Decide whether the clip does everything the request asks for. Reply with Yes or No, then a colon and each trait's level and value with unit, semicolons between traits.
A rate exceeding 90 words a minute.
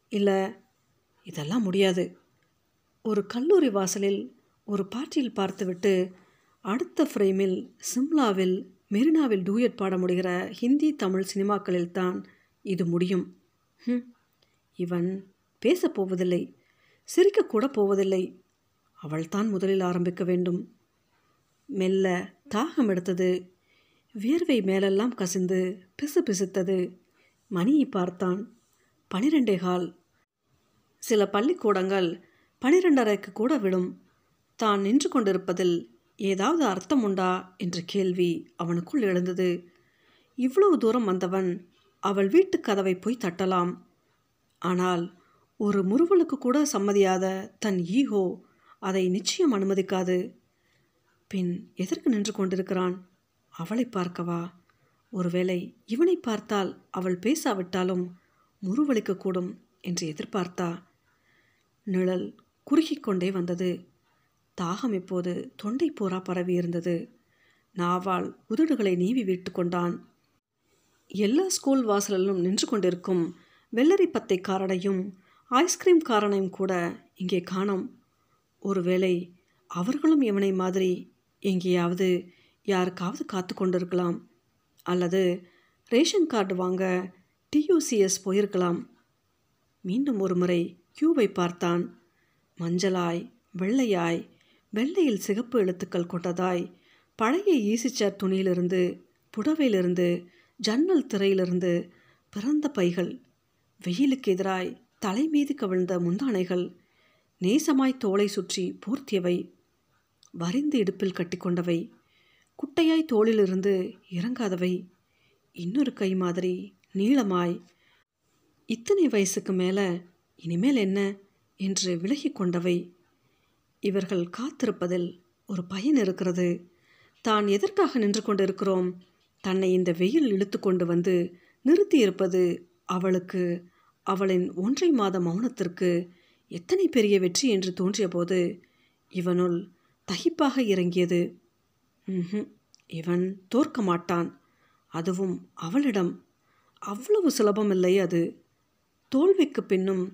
No: average, 85 wpm